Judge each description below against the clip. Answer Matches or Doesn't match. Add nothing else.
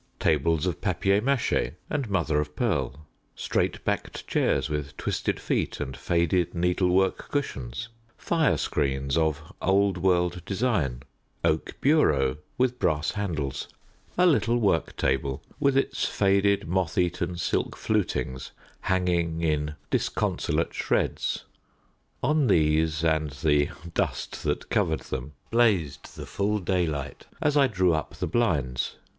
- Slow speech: Matches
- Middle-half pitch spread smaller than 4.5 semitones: Doesn't match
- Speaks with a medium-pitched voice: Doesn't match